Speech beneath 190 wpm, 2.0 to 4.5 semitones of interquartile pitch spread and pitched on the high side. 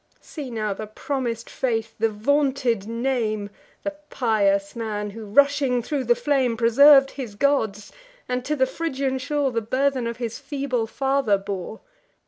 Yes: average, 150 wpm; average, 3.9 semitones; high, 240 Hz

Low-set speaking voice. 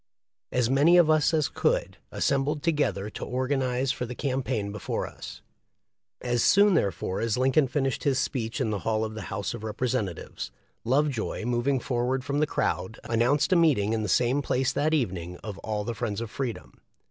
Yes: low, 125 Hz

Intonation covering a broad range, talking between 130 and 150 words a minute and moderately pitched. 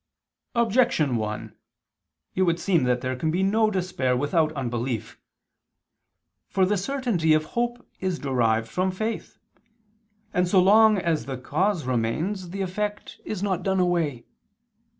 Yes: wide, 7.1 semitones; average, 140 wpm; medium, 180 Hz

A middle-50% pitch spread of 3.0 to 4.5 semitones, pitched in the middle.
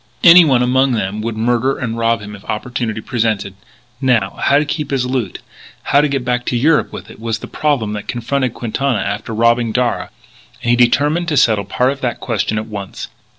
No: average, 3.6 semitones; low, 120 Hz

